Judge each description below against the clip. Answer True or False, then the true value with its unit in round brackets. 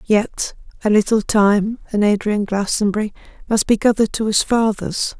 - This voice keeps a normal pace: True (150 wpm)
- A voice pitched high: True (210 Hz)